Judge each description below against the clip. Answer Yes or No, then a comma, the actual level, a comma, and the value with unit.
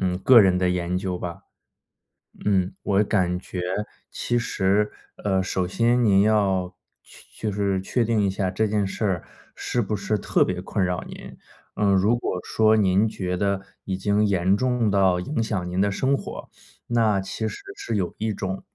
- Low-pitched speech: Yes, low, 100 Hz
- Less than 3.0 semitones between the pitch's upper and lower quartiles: Yes, narrow, 2.6 semitones